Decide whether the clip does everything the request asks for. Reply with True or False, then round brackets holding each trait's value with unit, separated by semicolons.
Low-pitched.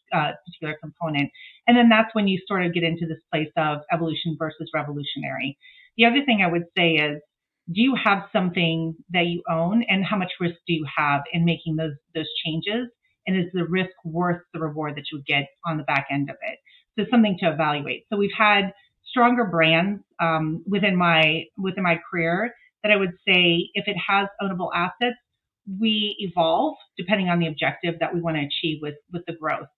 False (175 Hz)